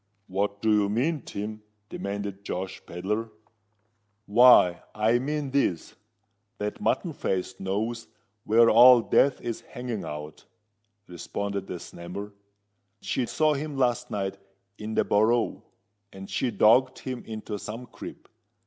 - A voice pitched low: Yes, low, 110 Hz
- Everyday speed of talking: No, slow, 125 wpm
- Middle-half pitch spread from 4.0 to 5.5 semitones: No, average, 3.6 semitones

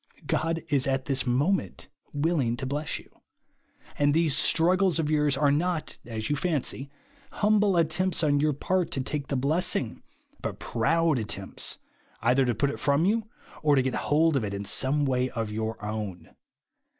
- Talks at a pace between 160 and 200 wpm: Yes, average, 175 wpm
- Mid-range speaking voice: Yes, medium, 145 Hz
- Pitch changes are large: No, average, 4.3 semitones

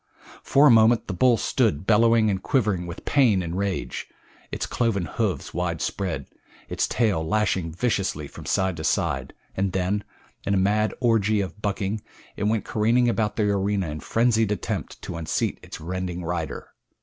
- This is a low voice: Yes, low, 100 Hz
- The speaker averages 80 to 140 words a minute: No, average, 165 wpm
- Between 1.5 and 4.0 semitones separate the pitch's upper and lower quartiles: Yes, average, 3.6 semitones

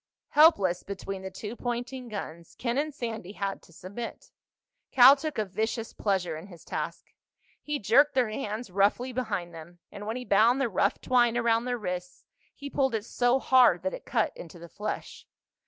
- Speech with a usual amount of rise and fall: Yes, average, 4.7 semitones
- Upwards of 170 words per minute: Yes, average, 185 wpm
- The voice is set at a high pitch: Yes, high, 220 Hz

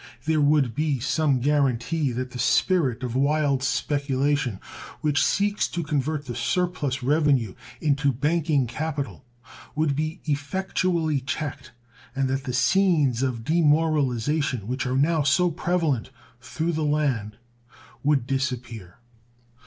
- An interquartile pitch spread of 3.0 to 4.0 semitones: Yes, average, 3.3 semitones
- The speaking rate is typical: No, slow, 125 wpm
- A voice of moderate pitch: Yes, medium, 145 Hz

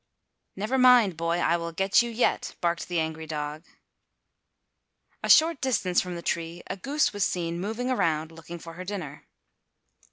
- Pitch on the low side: No, medium, 175 Hz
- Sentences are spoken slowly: No, average, 165 wpm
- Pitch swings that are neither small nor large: Yes, average, 4.7 semitones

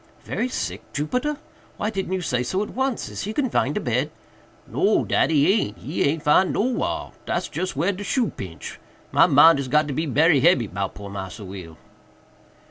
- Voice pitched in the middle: Yes, medium, 160 Hz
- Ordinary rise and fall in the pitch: No, wide, 8.4 semitones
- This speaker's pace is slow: No, average, 175 wpm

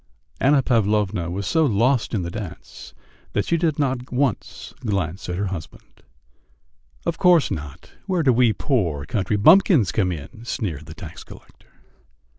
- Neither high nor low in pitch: No, low, 110 Hz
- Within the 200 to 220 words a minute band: No, average, 155 wpm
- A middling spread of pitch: No, wide, 7.0 semitones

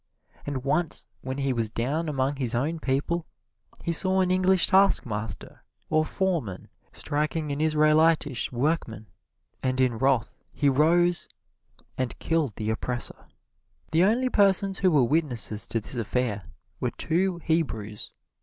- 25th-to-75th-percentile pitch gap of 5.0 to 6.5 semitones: Yes, wide, 5.4 semitones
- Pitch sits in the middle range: Yes, medium, 145 Hz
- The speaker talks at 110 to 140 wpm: Yes, slow, 135 wpm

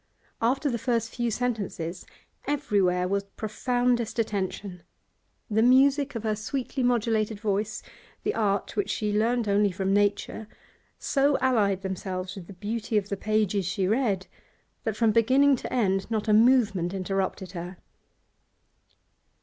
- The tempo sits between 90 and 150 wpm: Yes, average, 140 wpm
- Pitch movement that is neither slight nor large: Yes, average, 3.5 semitones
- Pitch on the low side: No, high, 215 Hz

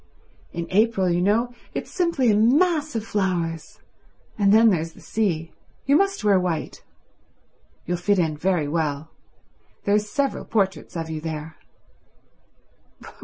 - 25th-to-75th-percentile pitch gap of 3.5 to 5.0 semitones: No, wide, 5.4 semitones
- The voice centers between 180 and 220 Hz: Yes, high, 190 Hz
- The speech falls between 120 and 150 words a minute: Yes, average, 140 wpm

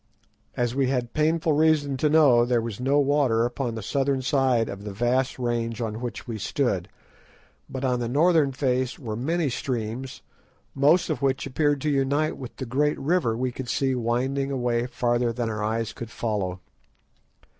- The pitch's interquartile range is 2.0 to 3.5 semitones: Yes, average, 3.1 semitones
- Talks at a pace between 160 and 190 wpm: Yes, average, 175 wpm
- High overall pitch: No, low, 125 Hz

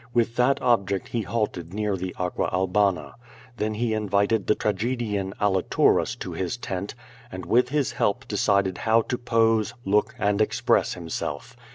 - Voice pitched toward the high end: No, low, 105 Hz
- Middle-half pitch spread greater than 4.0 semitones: No, average, 3.2 semitones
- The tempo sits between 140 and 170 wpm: Yes, average, 165 wpm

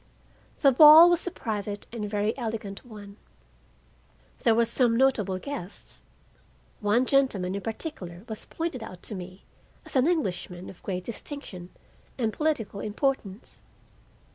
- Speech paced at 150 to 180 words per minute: No, slow, 135 wpm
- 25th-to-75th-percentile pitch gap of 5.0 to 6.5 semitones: Yes, average, 5.3 semitones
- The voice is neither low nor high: No, high, 220 Hz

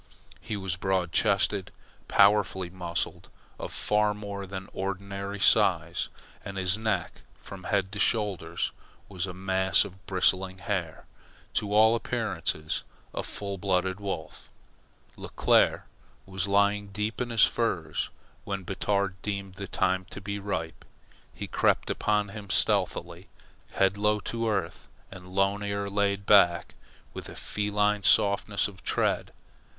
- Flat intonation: Yes, narrow, 1.6 semitones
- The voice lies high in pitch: No, low, 100 Hz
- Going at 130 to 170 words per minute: Yes, slow, 135 wpm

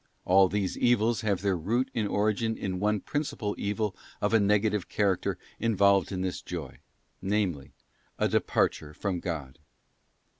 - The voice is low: Yes, low, 100 Hz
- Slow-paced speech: No, average, 145 wpm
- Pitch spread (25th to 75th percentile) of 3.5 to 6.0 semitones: No, narrow, 2.6 semitones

